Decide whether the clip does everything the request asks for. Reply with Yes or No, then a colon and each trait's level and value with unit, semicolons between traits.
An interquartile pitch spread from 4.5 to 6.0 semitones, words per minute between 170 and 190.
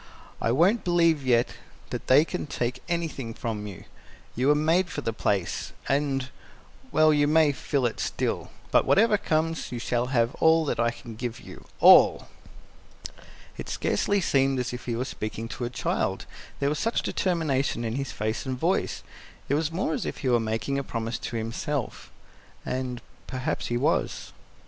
Yes: average, 4.8 semitones; average, 175 wpm